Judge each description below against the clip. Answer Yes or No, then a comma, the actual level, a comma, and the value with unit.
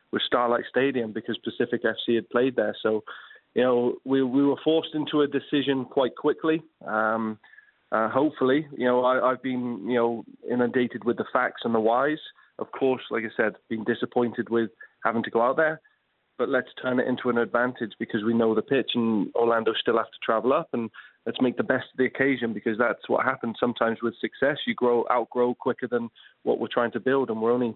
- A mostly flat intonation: Yes, narrow, 2.0 semitones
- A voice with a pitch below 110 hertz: No, low, 120 Hz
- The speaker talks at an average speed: No, fast, 210 wpm